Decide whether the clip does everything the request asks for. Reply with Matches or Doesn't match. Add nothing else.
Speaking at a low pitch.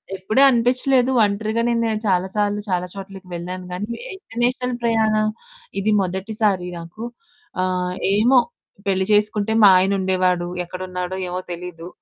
Doesn't match